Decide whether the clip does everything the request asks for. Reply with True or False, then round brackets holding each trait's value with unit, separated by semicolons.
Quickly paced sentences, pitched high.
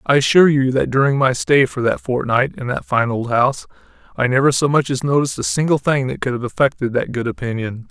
False (235 wpm; 130 Hz)